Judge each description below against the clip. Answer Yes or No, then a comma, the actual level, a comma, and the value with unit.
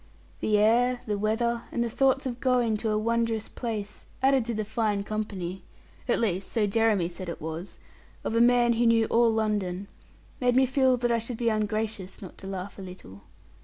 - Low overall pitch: No, high, 220 Hz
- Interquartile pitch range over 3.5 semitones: No, average, 2.8 semitones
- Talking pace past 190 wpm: Yes, average, 200 wpm